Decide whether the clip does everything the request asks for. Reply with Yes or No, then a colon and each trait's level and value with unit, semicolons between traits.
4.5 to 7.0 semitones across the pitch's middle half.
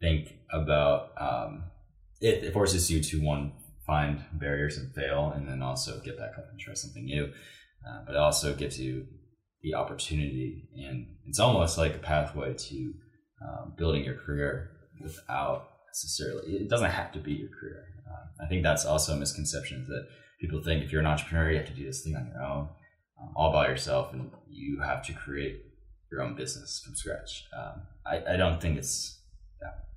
No: narrow, 2.6 semitones